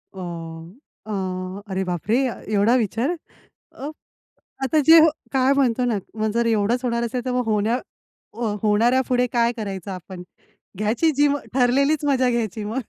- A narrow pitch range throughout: No, average, 3.9 semitones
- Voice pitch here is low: No, high, 230 Hz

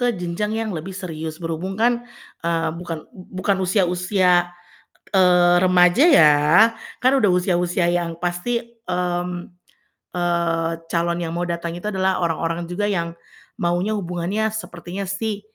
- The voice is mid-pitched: Yes, medium, 180 Hz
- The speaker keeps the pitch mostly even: Yes, narrow, 2.3 semitones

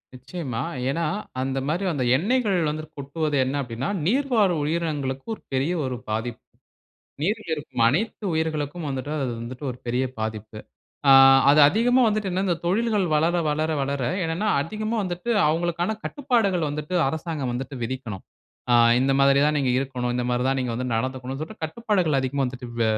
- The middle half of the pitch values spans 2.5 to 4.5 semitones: No, wide, 5.5 semitones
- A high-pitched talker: No, medium, 150 Hz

